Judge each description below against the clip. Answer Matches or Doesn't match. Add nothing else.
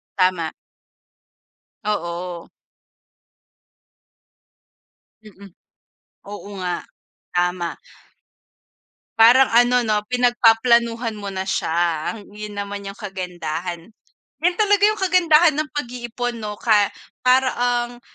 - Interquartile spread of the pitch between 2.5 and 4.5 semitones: Doesn't match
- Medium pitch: Doesn't match